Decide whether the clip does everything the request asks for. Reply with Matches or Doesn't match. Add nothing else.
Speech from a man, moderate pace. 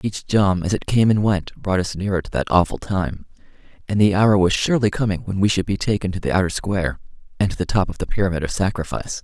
Doesn't match